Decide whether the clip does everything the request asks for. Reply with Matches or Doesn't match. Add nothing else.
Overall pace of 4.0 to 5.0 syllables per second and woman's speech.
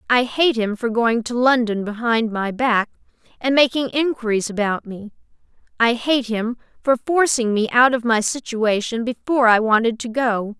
Matches